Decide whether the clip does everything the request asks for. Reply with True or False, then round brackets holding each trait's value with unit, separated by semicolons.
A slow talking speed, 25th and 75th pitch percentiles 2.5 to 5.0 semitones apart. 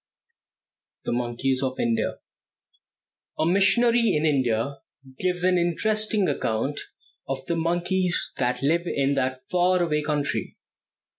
False (120 wpm; 5.4 semitones)